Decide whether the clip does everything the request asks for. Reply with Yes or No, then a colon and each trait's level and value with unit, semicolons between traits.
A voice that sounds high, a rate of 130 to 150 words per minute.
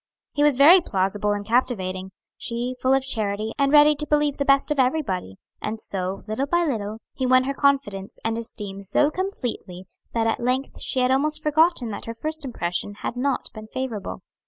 No: very high, 250 Hz; average, 190 wpm